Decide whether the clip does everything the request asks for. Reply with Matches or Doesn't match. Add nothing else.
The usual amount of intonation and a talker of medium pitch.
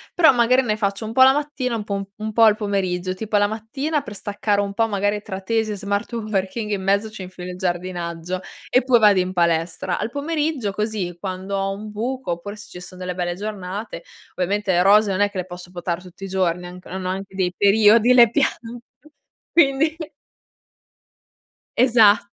Doesn't match